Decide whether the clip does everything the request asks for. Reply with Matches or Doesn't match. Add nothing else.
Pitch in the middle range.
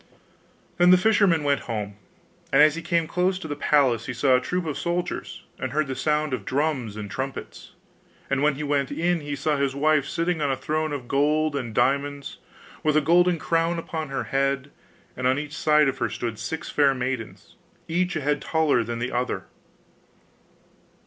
Matches